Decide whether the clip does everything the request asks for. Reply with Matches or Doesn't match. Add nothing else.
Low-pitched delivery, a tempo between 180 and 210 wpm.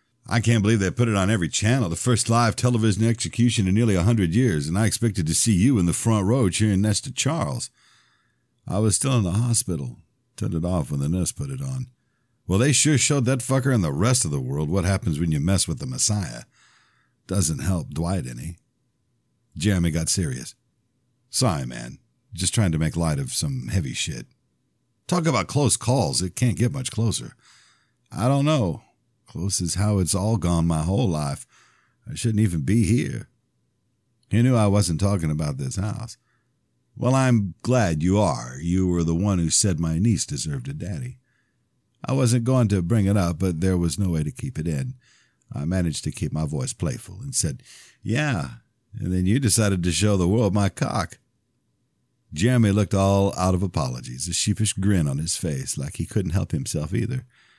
Matches